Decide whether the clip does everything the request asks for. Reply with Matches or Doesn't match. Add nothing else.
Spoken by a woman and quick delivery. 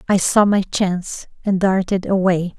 Doesn't match